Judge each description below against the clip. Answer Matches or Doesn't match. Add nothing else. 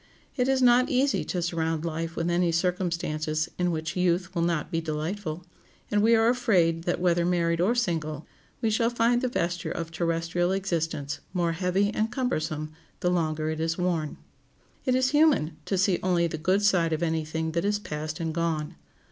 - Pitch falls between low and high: Matches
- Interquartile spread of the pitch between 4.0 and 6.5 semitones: Doesn't match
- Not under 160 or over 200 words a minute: Matches